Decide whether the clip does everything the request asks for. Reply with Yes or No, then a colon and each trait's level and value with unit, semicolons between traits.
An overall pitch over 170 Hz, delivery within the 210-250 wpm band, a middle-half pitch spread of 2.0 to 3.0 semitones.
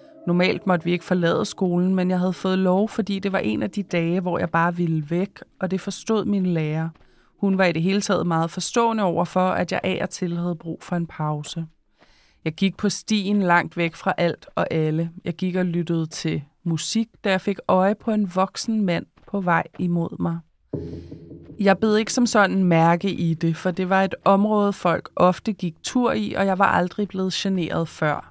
Yes: medium, 185 Hz; average, 215 wpm; average, 2.7 semitones